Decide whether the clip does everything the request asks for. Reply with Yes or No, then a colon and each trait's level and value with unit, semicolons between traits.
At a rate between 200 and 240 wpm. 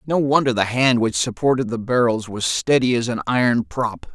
Yes: fast, 205 wpm